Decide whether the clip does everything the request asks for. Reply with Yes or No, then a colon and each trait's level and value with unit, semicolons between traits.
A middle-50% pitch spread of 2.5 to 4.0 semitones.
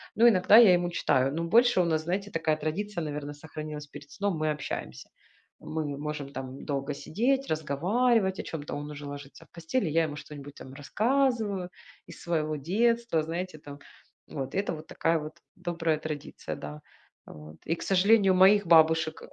No: average, 4.6 semitones